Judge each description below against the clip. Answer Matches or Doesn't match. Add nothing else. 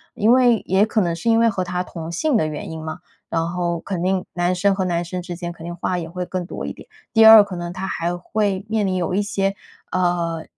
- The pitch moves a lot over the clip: Doesn't match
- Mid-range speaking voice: Matches